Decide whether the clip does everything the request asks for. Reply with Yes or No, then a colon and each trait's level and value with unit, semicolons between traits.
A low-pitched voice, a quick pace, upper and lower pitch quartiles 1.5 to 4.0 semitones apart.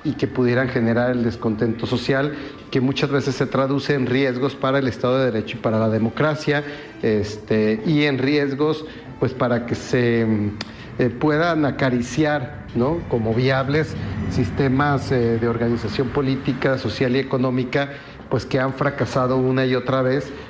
No: low, 130 Hz; average, 155 wpm; average, 2.8 semitones